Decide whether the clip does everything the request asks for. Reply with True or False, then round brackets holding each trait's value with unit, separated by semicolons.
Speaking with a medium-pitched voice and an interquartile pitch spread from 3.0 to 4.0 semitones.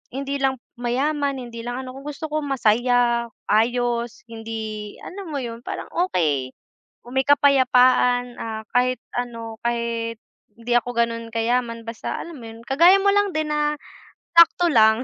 False (245 Hz; 3.3 semitones)